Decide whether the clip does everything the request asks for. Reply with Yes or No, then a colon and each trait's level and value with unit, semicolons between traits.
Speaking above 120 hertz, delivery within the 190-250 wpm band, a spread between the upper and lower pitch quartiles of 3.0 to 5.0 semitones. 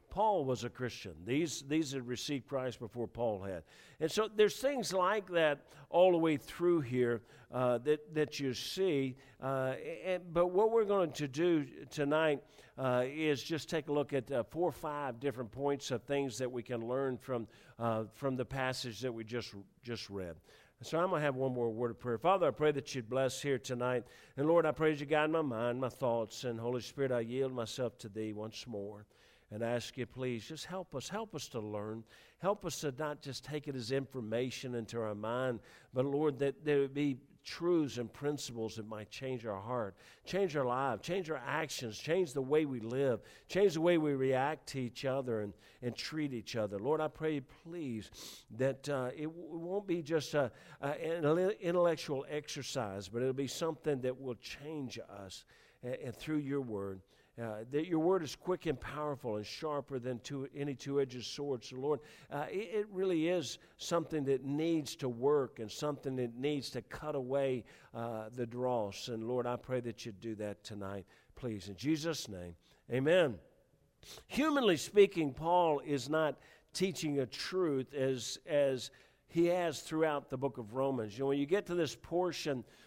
Yes: low, 135 Hz; average, 200 wpm; average, 4.1 semitones